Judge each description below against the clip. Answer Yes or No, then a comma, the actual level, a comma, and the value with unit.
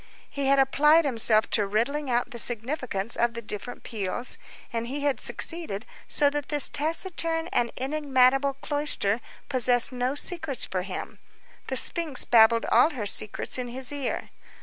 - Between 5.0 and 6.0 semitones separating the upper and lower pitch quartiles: No, average, 3.8 semitones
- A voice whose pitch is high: Yes, very high, 255 Hz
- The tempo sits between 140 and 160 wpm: Yes, average, 155 wpm